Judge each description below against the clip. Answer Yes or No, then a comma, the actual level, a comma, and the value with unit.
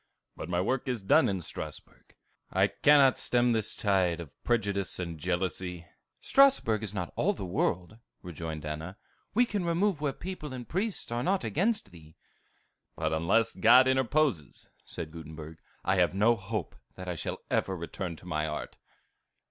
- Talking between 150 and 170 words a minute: Yes, average, 165 wpm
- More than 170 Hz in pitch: No, low, 100 Hz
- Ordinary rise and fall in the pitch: No, wide, 7.2 semitones